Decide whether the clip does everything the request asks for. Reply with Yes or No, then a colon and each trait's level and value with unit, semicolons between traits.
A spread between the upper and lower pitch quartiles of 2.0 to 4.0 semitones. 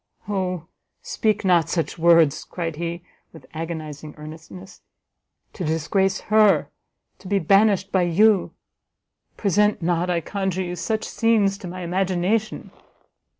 Yes: average, 3.0 semitones